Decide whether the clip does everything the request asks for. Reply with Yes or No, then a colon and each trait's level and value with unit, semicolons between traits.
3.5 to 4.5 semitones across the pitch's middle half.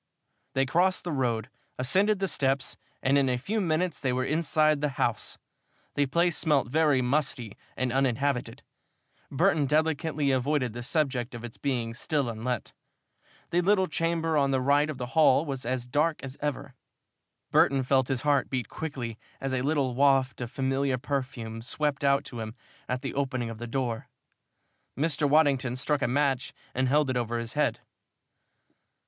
No: average, 3.1 semitones